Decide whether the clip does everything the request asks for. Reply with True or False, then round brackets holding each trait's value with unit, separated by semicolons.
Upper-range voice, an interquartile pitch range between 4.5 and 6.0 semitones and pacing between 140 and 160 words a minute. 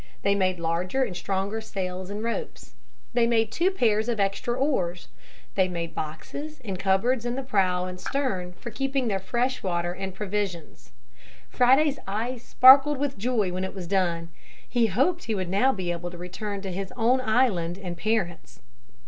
False (200 Hz; 5.1 semitones; 175 wpm)